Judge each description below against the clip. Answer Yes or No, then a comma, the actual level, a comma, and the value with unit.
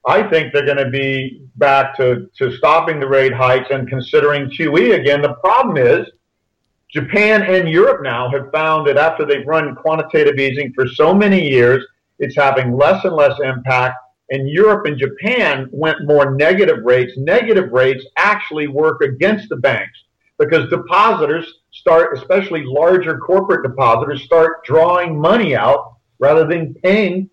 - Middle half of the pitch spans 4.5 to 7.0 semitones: No, average, 4.0 semitones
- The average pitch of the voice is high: No, medium, 145 Hz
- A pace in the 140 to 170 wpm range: Yes, average, 155 wpm